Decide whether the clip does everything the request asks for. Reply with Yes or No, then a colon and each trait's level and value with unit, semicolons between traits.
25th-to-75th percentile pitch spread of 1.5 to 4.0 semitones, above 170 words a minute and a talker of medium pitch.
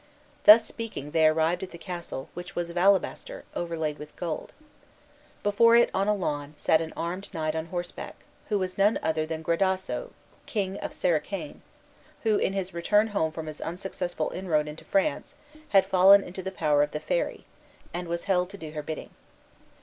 Yes: average, 3.6 semitones; average, 180 wpm; medium, 175 Hz